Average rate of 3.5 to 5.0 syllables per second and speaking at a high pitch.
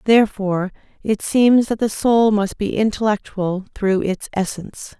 Yes: 4.6 syllables/s; high, 205 Hz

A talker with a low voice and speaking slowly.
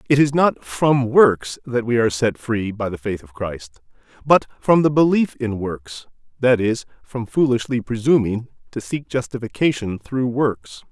No: low, 120 Hz; average, 170 wpm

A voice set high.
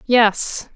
Yes: high, 225 Hz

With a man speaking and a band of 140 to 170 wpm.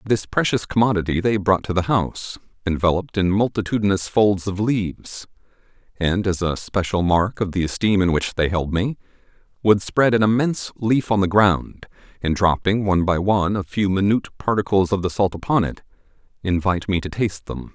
No: male; average, 185 wpm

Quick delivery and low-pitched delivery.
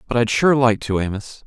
Yes: fast, 245 wpm; low, 115 Hz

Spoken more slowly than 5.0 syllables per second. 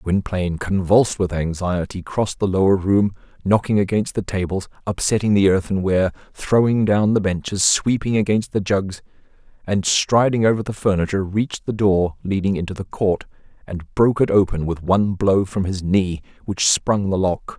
No: 5.1 syllables/s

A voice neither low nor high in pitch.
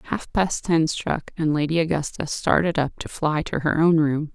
Yes: medium, 160 Hz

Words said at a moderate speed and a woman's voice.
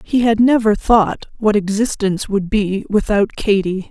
Yes: average, 155 wpm; female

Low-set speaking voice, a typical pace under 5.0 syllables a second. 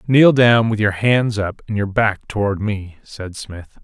Yes: low, 105 Hz; 3.9 syllables/s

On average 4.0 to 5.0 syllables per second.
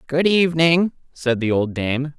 Yes: 4.4 syllables/s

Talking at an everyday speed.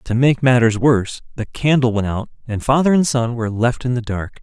No: fast, 230 wpm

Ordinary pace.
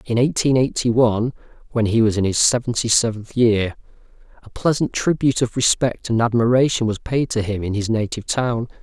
Yes: average, 185 wpm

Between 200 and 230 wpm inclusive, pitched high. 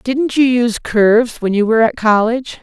Yes: fast, 205 wpm; high, 235 Hz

